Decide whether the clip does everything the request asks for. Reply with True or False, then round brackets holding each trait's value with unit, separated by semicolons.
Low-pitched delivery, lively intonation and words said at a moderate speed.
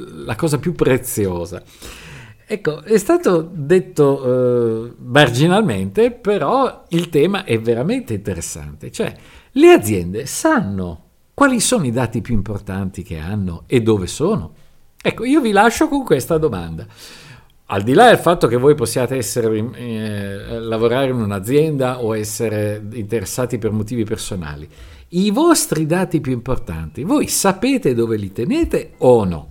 True (125 Hz; 8.3 semitones; 140 wpm)